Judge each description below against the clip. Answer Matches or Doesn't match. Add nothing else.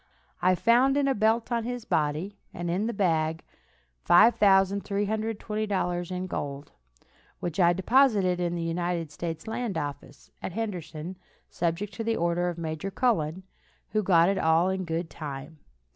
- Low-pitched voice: Doesn't match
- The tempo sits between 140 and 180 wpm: Matches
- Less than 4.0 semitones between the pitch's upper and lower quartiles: Doesn't match